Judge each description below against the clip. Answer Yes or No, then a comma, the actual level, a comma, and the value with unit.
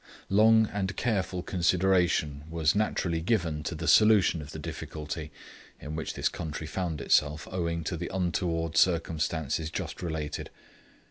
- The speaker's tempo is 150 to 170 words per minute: No, average, 140 wpm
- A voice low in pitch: Yes, very low, 85 Hz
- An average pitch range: Yes, average, 3.1 semitones